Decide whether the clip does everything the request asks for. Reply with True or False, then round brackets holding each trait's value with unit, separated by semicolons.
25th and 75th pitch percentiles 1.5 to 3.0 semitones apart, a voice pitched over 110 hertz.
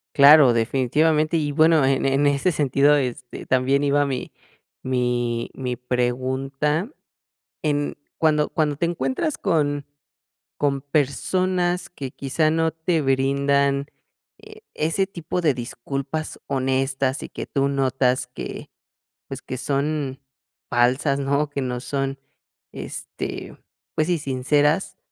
True (2.7 semitones; 140 Hz)